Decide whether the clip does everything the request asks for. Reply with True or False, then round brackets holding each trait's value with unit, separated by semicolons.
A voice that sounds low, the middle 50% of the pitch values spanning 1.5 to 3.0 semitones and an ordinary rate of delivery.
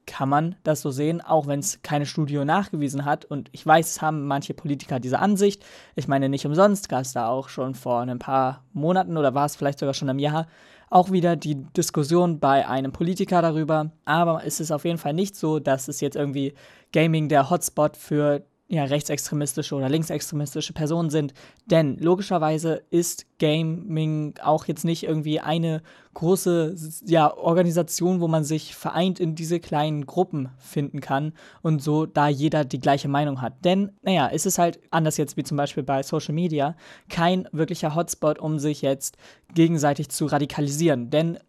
False (155 Hz; 2.6 semitones; 180 wpm)